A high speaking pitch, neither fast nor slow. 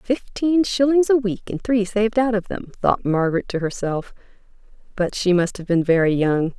Yes: high, 205 Hz; average, 190 wpm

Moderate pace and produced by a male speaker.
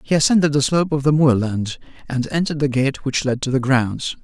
No: fast, 225 wpm; male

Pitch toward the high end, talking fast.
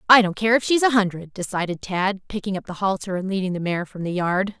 Yes: high, 195 Hz; fast, 260 wpm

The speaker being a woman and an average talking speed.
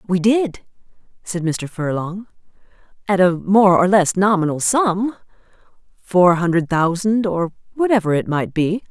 No: female; slow, 130 wpm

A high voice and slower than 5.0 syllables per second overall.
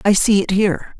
No: high, 195 Hz; 5.8 syllables/s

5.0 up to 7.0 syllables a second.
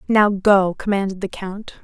No: 4.6 syllables/s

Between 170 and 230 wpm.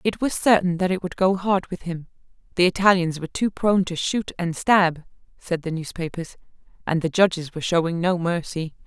Yes: average, 195 wpm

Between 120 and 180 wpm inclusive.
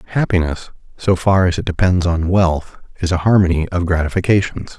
Yes: average, 165 wpm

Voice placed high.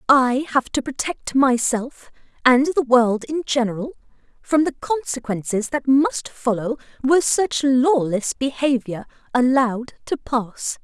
Yes: very high, 255 Hz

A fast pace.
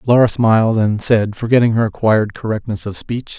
No: average, 175 wpm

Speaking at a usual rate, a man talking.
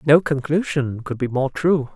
Yes: average, 185 wpm; male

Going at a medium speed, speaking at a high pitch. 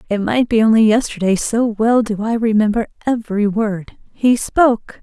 Yes: average, 165 wpm; high, 220 Hz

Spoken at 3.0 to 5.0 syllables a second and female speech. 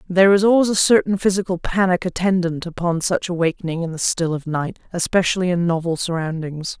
No: 5.9 syllables/s; female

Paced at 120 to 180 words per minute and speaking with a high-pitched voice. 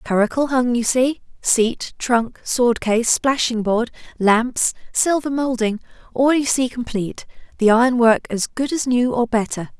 Yes: average, 160 wpm; high, 240 Hz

